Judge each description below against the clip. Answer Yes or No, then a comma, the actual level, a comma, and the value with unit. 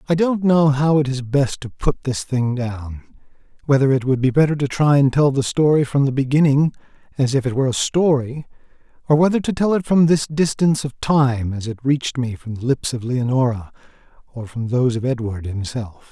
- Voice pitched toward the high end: No, low, 135 Hz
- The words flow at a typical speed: No, fast, 210 wpm